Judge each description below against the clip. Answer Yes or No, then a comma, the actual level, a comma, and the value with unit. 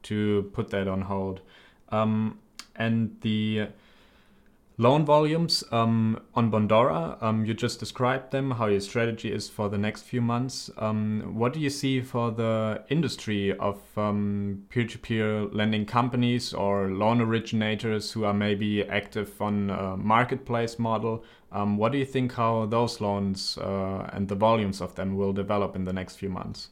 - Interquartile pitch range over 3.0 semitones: No, narrow, 2.4 semitones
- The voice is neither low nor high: No, low, 110 Hz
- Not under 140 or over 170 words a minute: Yes, average, 160 wpm